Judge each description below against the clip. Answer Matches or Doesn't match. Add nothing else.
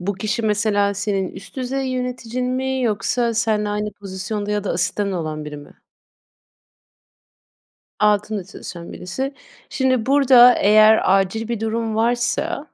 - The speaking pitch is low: Doesn't match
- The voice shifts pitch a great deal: Doesn't match